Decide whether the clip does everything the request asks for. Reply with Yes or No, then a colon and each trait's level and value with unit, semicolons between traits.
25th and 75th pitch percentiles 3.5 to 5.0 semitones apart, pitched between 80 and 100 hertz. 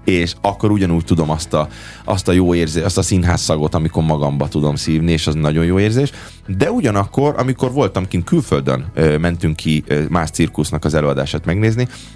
Yes: average, 4.2 semitones; very low, 85 Hz